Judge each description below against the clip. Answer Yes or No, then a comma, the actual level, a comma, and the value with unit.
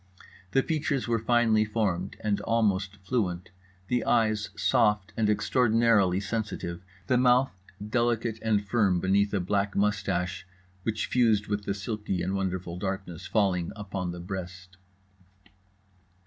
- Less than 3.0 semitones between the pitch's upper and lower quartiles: No, average, 3.3 semitones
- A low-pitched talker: Yes, low, 105 Hz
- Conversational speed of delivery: No, slow, 130 wpm